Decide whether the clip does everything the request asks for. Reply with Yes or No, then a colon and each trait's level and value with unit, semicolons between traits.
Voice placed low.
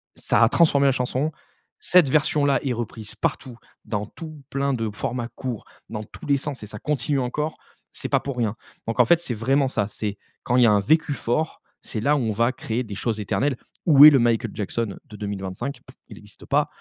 Yes: low, 125 Hz